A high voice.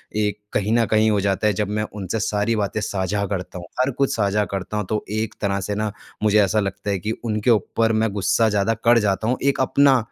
No: low, 105 Hz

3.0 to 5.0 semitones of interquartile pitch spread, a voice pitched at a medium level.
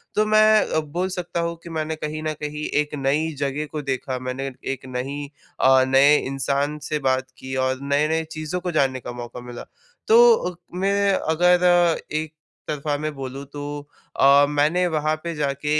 Yes: average, 3.6 semitones; medium, 150 Hz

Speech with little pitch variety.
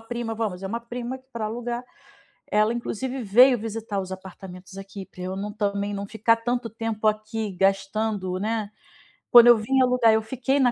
No: average, 3.0 semitones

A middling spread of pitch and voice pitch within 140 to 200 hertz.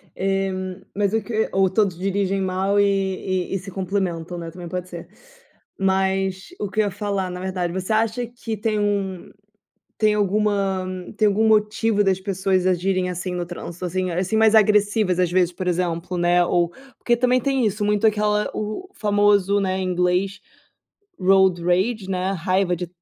No: narrow, 2.3 semitones; high, 190 Hz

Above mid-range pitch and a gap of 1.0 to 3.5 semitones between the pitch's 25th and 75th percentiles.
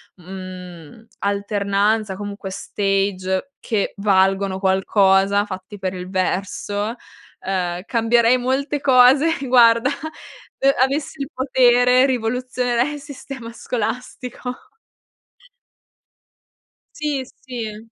No: high, 220 Hz; average, 4.7 semitones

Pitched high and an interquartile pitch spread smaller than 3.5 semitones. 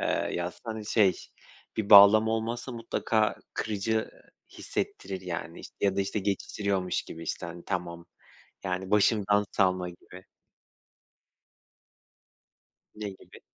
No: low, 100 Hz; average, 2.8 semitones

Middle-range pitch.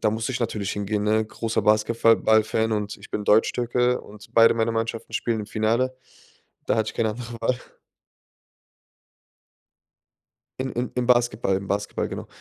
No: low, 110 Hz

